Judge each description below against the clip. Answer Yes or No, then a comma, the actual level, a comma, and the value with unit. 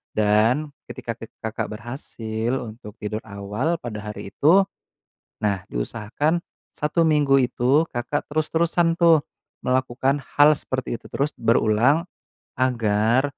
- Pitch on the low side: Yes, low, 125 Hz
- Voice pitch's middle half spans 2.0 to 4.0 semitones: No, average, 5.2 semitones